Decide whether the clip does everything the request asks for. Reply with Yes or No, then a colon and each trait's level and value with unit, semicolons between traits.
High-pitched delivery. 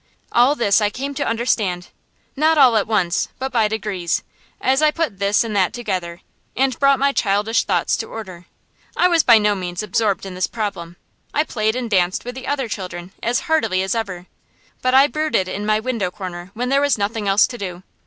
Yes: high, 215 Hz